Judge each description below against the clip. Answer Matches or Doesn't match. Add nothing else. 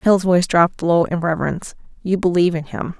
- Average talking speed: Matches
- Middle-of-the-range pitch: Matches